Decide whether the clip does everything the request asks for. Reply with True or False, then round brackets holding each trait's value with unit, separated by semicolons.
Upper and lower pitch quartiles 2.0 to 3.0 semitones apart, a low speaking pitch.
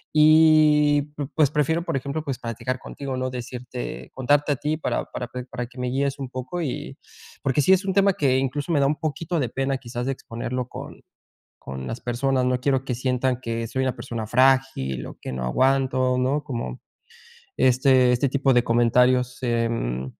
True (2.4 semitones; 130 Hz)